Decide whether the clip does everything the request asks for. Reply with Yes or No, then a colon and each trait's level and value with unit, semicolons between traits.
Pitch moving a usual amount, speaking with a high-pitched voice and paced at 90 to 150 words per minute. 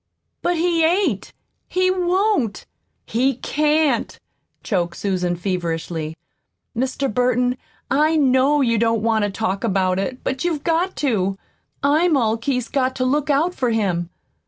No: wide, 7.0 semitones; very high, 255 Hz; average, 140 wpm